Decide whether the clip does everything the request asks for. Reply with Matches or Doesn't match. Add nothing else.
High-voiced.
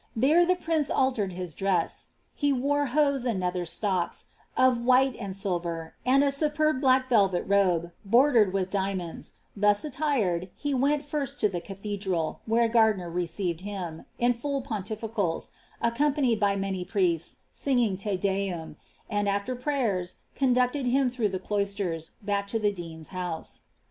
Matches